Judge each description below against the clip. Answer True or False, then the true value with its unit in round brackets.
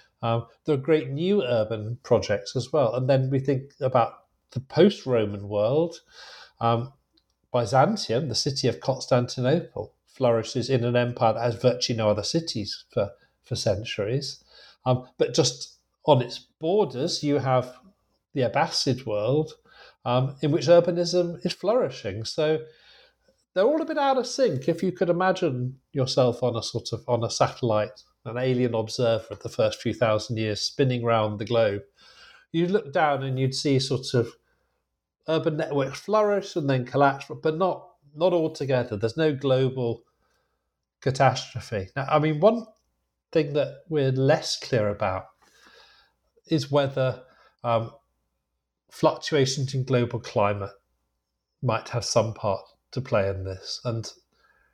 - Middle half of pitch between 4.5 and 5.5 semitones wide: True (5.2 semitones)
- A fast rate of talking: False (150 wpm)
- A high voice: False (130 Hz)